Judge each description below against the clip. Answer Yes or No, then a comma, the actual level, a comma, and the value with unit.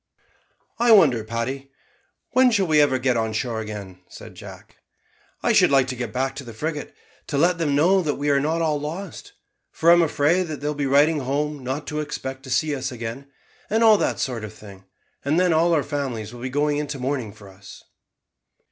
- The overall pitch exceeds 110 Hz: Yes, medium, 140 Hz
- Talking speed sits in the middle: No, fast, 210 wpm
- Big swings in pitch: No, average, 4.1 semitones